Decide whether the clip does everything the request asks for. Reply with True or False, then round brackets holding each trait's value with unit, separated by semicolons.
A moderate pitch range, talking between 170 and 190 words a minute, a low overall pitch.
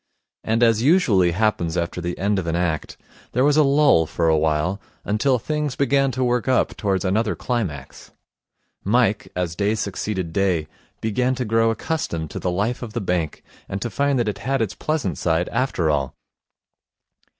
False (6.1 semitones; 180 wpm; 105 Hz)